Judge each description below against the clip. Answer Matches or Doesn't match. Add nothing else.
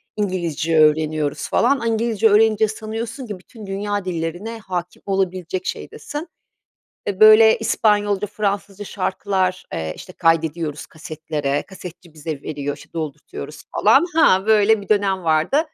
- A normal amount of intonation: Matches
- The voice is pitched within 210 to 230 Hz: Doesn't match